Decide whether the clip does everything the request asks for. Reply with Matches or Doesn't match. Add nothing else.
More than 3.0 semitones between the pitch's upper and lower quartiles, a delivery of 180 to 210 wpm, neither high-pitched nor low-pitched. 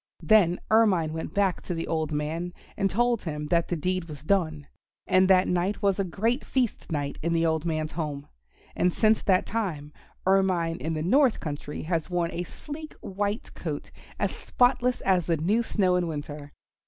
Matches